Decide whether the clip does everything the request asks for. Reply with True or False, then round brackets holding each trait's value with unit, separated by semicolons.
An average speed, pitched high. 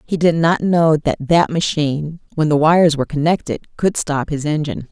False (195 wpm; 155 Hz)